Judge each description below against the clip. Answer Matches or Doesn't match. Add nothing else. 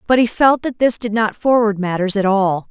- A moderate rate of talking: Doesn't match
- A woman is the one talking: Matches